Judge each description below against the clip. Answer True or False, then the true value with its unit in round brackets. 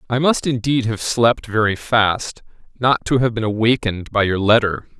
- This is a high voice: False (115 Hz)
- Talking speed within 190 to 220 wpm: False (180 wpm)